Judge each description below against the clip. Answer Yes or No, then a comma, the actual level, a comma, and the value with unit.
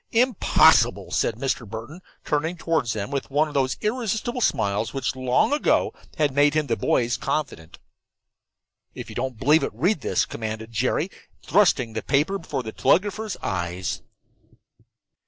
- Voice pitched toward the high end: No, medium, 140 Hz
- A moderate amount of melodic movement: No, wide, 7.0 semitones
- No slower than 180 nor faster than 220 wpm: No, average, 150 wpm